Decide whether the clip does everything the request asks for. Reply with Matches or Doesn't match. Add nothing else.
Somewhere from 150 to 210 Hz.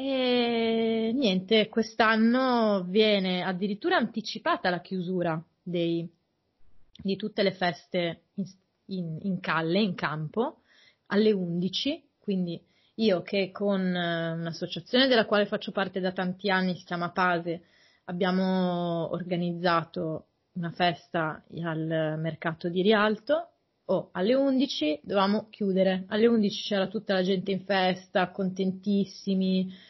Matches